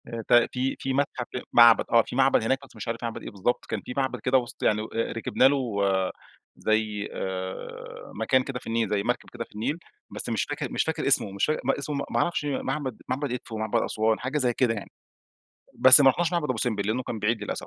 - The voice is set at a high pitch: No, low, 120 Hz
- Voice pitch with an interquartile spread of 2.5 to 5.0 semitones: Yes, average, 3.4 semitones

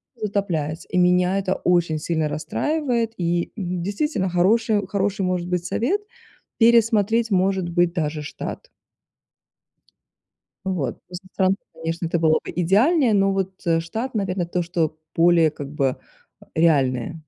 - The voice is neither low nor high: Yes, medium, 180 Hz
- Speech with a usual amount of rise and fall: Yes, average, 3.5 semitones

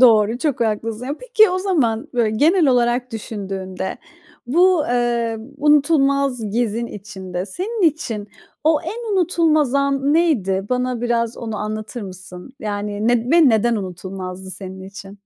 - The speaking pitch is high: Yes, high, 235 Hz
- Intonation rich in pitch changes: Yes, wide, 5.8 semitones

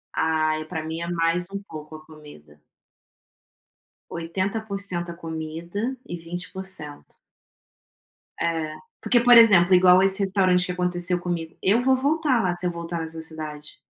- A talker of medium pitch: Yes, medium, 175 Hz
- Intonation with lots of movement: No, average, 3.0 semitones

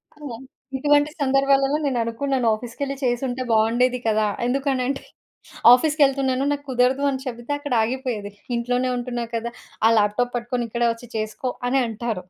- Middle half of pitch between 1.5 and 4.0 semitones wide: Yes, narrow, 2.5 semitones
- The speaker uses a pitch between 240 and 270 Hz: Yes, very high, 250 Hz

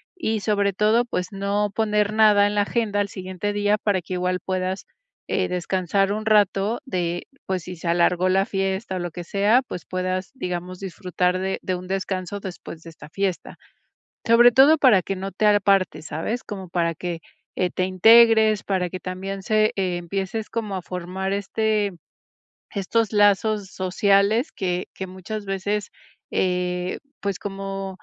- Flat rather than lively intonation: Yes, narrow, 2.2 semitones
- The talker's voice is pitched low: No, high, 195 Hz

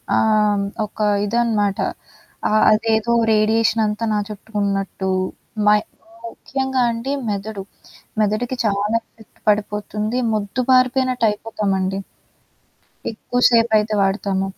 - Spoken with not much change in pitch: Yes, narrow, 2.0 semitones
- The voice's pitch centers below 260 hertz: Yes, high, 215 Hz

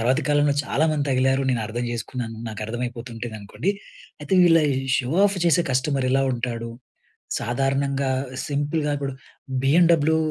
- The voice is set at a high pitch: No, low, 135 Hz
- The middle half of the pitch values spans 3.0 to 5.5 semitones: Yes, average, 3.4 semitones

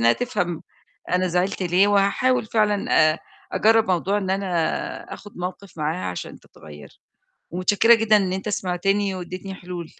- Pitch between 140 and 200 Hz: Yes, high, 190 Hz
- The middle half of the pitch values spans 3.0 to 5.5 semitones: No, narrow, 2.5 semitones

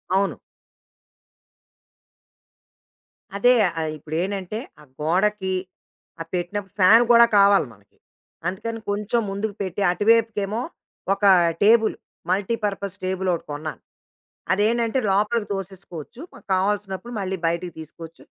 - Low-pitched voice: No, high, 195 Hz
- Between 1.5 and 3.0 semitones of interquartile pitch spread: Yes, average, 2.7 semitones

